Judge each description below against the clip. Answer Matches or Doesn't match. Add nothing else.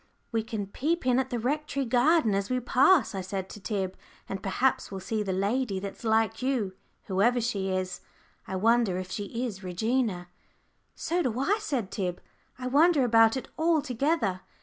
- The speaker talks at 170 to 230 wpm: Matches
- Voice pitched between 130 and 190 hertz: Doesn't match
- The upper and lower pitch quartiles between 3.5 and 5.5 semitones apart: Matches